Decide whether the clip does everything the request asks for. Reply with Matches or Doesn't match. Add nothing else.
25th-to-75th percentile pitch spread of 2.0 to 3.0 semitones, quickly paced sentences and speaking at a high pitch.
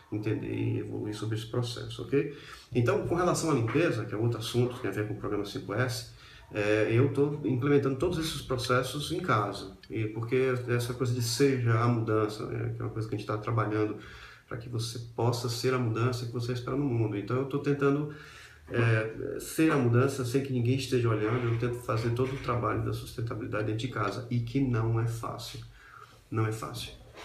Doesn't match